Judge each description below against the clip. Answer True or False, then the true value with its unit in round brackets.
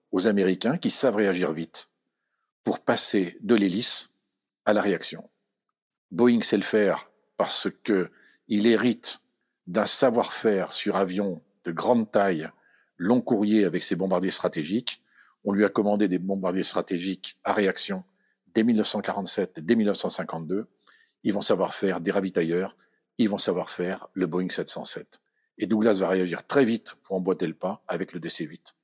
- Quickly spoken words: False (155 wpm)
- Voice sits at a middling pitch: False (100 Hz)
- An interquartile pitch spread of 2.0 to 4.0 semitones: True (3.4 semitones)